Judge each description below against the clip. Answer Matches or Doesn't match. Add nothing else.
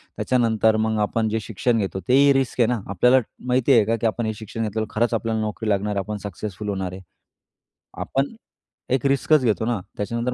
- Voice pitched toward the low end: Matches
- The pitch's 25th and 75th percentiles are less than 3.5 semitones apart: Matches